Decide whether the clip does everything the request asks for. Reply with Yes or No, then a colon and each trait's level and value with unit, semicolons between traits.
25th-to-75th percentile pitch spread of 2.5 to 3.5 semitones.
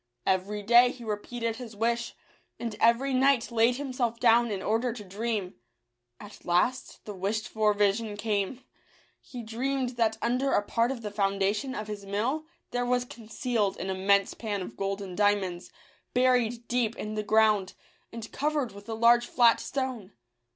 Yes: average, 3.0 semitones